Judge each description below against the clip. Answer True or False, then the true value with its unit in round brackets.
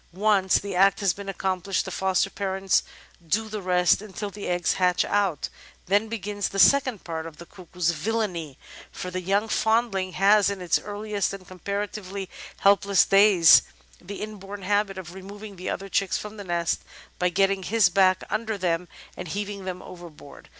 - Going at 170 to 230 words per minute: True (175 wpm)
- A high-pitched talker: True (195 Hz)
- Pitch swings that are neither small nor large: False (2.2 semitones)